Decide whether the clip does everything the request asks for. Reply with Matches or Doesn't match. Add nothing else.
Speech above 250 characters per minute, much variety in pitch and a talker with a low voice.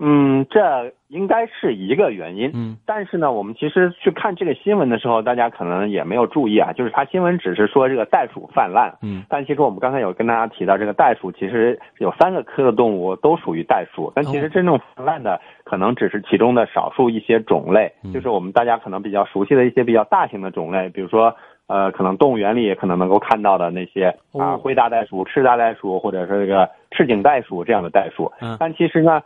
Matches